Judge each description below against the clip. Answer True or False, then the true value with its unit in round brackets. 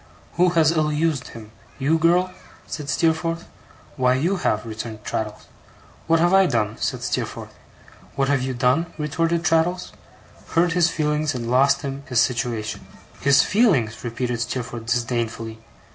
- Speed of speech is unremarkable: True (145 wpm)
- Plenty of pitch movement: True (5.8 semitones)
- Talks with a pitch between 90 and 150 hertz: True (140 Hz)